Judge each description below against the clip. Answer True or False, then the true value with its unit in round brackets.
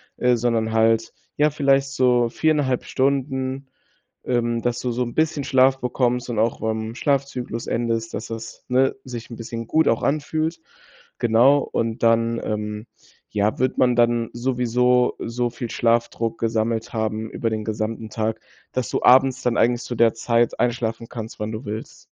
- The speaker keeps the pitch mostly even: True (2.2 semitones)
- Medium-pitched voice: False (120 Hz)